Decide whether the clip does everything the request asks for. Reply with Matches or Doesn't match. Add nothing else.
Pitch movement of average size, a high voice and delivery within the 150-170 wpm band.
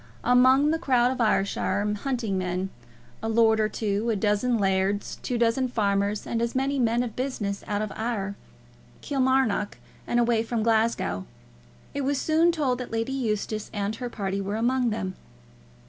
Matches